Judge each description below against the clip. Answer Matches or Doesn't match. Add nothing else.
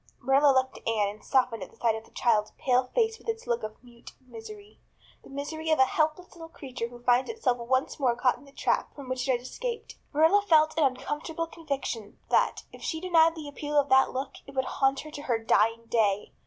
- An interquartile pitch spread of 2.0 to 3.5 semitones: Doesn't match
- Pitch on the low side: Doesn't match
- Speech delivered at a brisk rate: Matches